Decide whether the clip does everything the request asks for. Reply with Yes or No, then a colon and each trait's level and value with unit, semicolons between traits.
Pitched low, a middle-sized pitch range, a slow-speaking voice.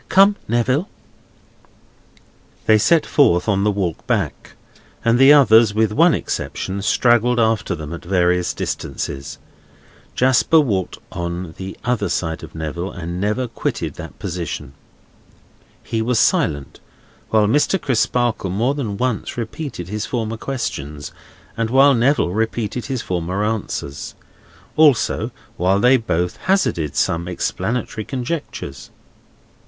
No: low, 110 Hz; wide, 5.9 semitones; slow, 125 wpm